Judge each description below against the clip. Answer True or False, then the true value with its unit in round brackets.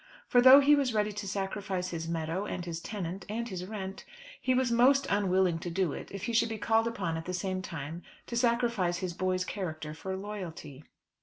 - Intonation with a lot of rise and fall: False (4.3 semitones)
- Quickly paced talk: True (210 wpm)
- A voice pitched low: False (190 Hz)